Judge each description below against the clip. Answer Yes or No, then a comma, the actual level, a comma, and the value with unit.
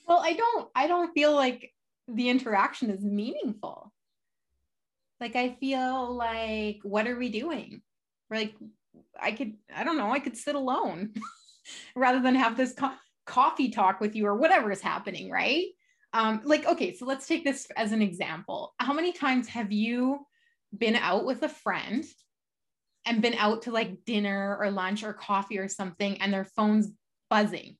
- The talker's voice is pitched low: No, high, 235 Hz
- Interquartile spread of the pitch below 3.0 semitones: No, average, 4.7 semitones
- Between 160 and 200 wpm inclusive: Yes, average, 175 wpm